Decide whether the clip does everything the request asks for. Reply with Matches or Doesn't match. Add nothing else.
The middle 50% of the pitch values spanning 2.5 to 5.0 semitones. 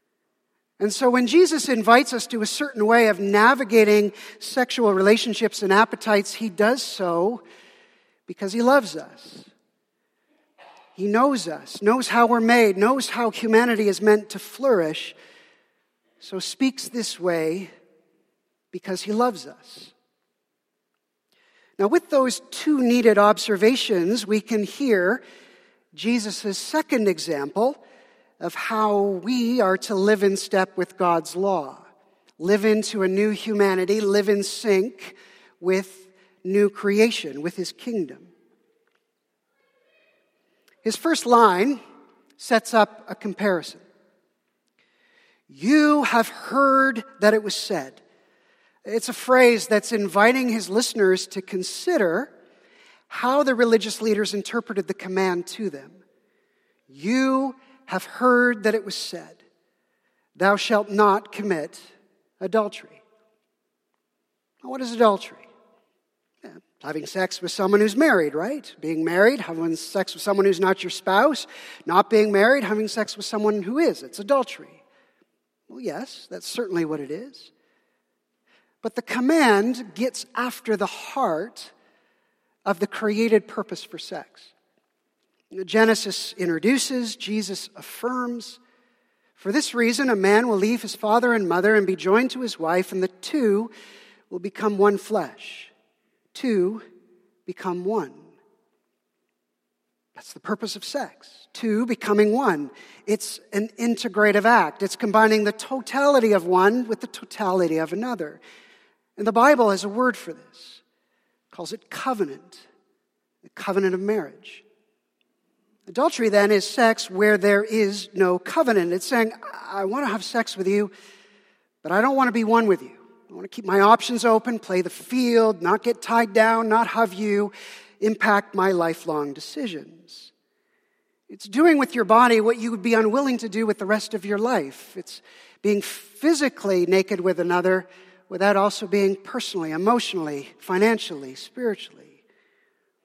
Matches